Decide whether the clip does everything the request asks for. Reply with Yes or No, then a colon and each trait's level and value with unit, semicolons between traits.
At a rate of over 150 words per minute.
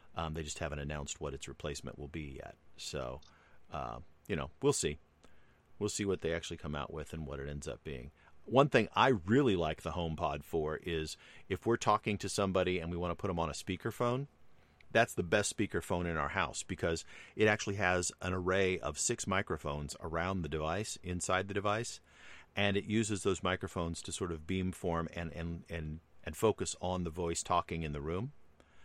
Yes: fast, 205 wpm